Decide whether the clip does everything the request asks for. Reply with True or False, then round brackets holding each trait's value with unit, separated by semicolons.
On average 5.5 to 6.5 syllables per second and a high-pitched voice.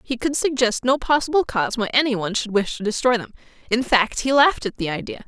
True (6.1 syllables/s; 240 Hz)